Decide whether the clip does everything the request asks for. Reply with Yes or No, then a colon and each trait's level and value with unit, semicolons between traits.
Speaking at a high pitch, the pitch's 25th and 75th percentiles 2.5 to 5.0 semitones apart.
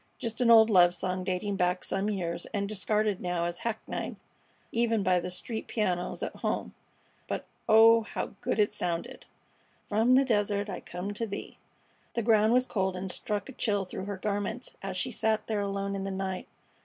Yes: high, 200 Hz; average, 3.0 semitones